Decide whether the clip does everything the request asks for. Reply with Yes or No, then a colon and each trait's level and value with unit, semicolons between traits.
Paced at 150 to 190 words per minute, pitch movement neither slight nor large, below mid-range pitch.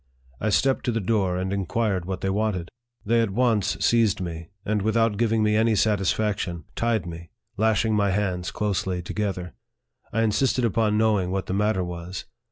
Yes: average, 175 wpm; average, 3.1 semitones; low, 105 Hz